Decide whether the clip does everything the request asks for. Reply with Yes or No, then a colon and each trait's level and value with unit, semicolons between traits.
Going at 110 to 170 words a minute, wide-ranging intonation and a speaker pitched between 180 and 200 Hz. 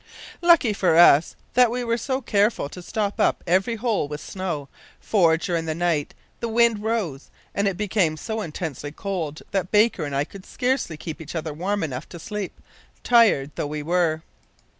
No: average, 185 wpm; wide, 5.7 semitones; medium, 185 Hz